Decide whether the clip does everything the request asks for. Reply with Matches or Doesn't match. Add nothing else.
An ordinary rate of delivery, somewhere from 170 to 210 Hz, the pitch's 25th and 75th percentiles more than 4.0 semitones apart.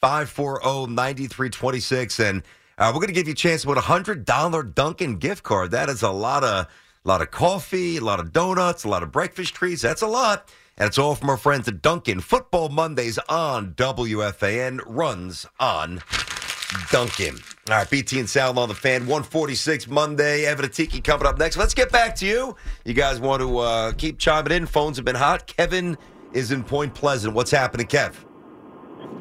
Doesn't match